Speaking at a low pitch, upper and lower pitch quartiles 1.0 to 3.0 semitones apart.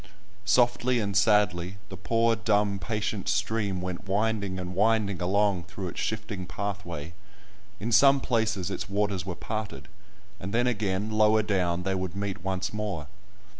Yes: low, 100 Hz; narrow, 2.6 semitones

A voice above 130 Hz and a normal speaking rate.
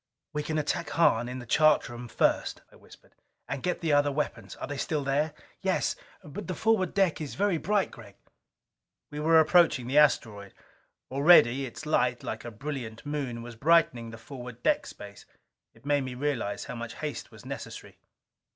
Yes: medium, 140 Hz; average, 180 wpm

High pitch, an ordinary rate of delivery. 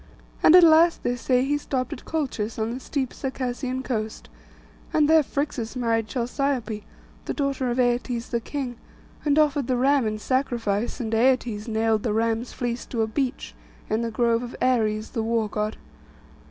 Yes: high, 245 Hz; average, 175 wpm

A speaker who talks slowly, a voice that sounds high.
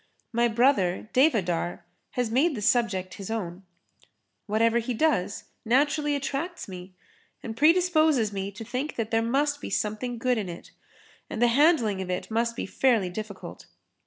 No: average, 160 wpm; high, 230 Hz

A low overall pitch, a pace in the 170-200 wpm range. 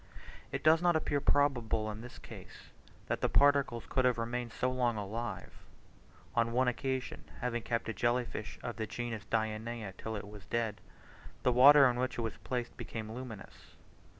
Yes: low, 120 Hz; average, 180 wpm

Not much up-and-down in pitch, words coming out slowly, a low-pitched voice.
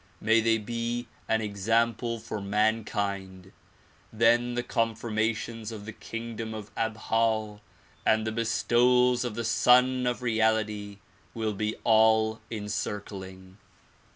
Yes: narrow, 1.6 semitones; slow, 115 wpm; low, 110 Hz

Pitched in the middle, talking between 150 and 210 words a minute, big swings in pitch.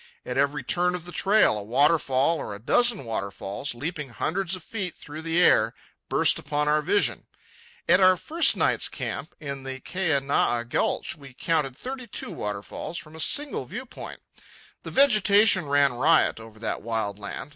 Yes: medium, 150 Hz; average, 165 wpm; wide, 6.7 semitones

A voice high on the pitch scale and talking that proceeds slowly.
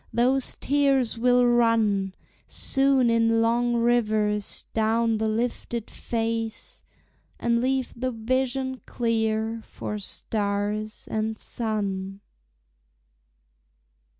Yes: high, 230 Hz; slow, 90 wpm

